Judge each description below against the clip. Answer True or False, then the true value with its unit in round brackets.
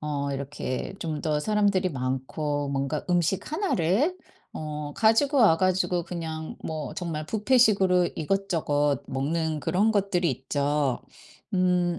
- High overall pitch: False (165 Hz)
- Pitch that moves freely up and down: False (4.6 semitones)